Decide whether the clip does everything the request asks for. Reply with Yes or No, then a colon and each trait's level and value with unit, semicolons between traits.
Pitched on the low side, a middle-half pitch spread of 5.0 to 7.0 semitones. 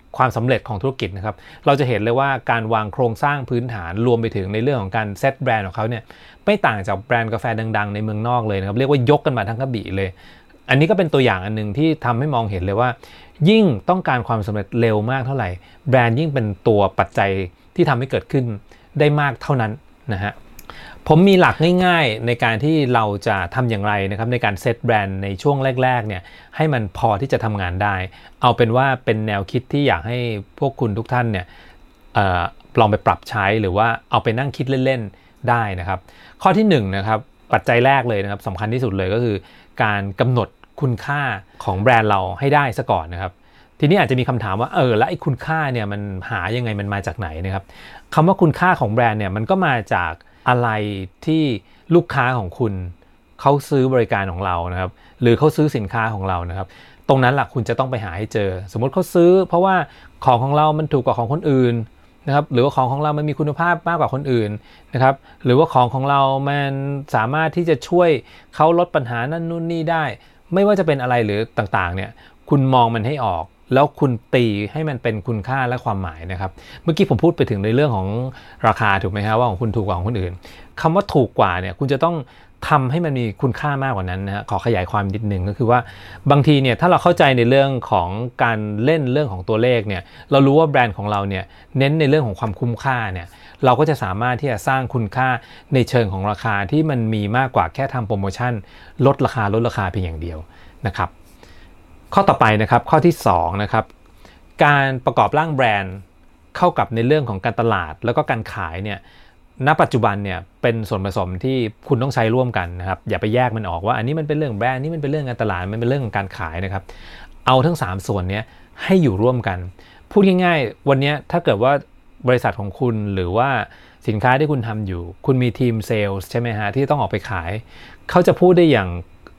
Yes: low, 120 Hz; wide, 5.4 semitones